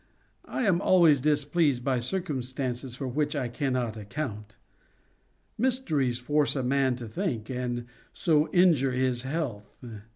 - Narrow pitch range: No, average, 3.8 semitones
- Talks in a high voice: No, low, 135 Hz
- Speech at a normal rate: No, slow, 130 wpm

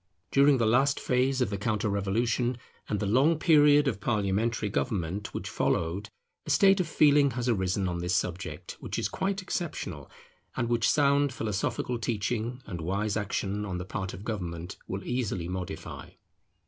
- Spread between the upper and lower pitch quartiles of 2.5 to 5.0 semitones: No, wide, 5.4 semitones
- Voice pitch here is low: Yes, low, 110 Hz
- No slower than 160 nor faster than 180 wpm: Yes, average, 165 wpm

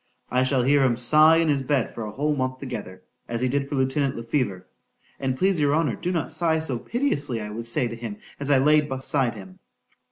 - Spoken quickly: Yes, fast, 230 wpm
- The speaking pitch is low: Yes, low, 130 Hz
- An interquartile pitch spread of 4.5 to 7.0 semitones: No, average, 4.0 semitones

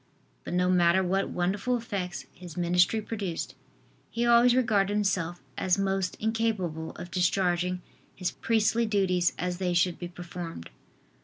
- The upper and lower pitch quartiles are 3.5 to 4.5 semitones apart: No, average, 2.8 semitones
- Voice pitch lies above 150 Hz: Yes, medium, 185 Hz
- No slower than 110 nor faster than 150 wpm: Yes, average, 140 wpm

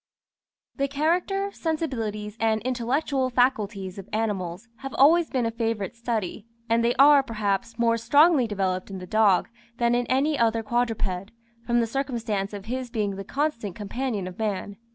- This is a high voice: Yes, high, 230 Hz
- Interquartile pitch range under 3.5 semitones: No, average, 4.2 semitones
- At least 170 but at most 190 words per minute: No, average, 160 wpm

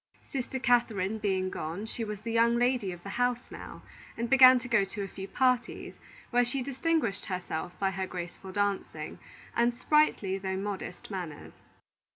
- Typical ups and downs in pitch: Yes, average, 4.3 semitones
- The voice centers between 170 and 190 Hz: No, high, 210 Hz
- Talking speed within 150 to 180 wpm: Yes, average, 170 wpm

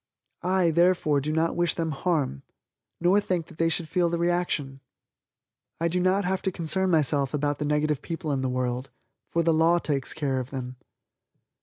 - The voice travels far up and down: No, average, 3.6 semitones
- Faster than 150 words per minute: Yes, average, 185 wpm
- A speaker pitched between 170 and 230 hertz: No, medium, 160 Hz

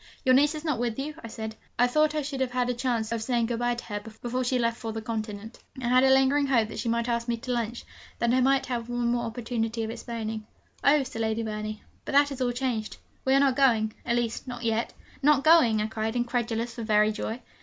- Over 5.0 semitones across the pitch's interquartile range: No, narrow, 2.4 semitones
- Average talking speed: No, fast, 255 wpm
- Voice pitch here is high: Yes, high, 240 Hz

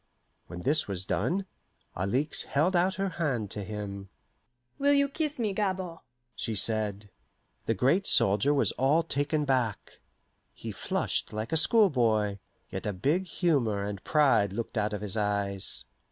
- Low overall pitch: Yes, low, 125 Hz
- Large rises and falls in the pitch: Yes, wide, 8.4 semitones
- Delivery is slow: No, average, 155 wpm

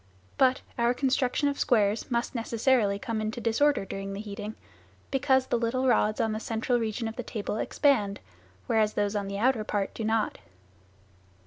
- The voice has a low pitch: No, high, 225 Hz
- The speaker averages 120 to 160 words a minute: No, average, 175 wpm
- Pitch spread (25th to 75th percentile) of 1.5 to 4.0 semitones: Yes, average, 3.2 semitones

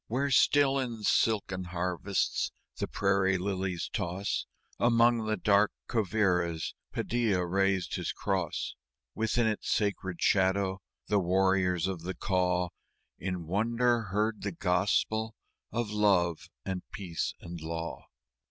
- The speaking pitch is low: Yes, very low, 95 Hz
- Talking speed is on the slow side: Yes, slow, 120 wpm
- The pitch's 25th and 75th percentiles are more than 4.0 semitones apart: No, average, 3.2 semitones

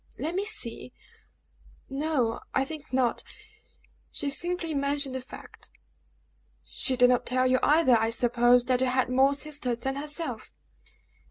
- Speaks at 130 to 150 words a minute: Yes, average, 145 wpm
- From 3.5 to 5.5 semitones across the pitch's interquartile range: No, average, 3.0 semitones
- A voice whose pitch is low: No, very high, 265 Hz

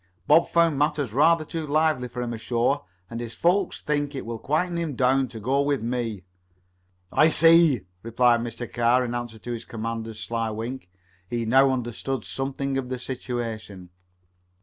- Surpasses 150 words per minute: Yes, average, 170 wpm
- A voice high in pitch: No, low, 125 Hz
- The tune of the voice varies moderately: Yes, average, 3.9 semitones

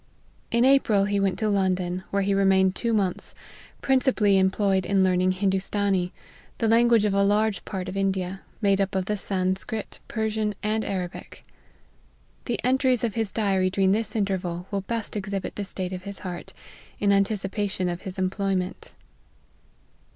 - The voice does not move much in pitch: Yes, narrow, 2.0 semitones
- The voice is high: Yes, high, 195 Hz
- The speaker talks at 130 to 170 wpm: Yes, average, 160 wpm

